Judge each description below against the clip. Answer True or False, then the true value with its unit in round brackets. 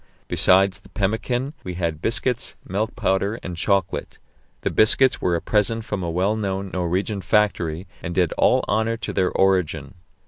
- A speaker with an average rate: True (165 wpm)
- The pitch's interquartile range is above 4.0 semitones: False (3.4 semitones)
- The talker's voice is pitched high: False (95 Hz)